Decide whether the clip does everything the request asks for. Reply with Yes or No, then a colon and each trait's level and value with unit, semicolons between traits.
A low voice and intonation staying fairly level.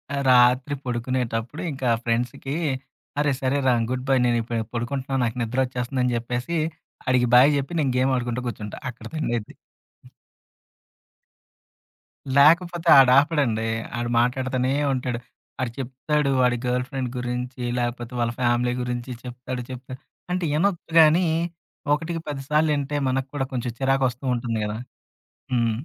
Yes: low, 125 Hz; narrow, 2.2 semitones